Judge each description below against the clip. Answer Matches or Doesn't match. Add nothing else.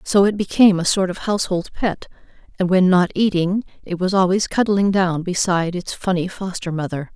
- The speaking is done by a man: Doesn't match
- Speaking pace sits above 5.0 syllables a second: Matches